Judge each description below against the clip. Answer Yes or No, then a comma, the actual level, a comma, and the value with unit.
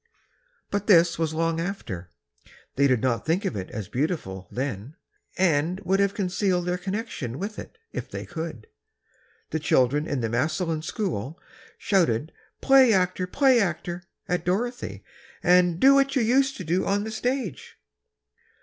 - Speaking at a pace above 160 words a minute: No, average, 155 wpm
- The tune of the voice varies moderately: No, wide, 5.7 semitones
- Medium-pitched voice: Yes, medium, 175 Hz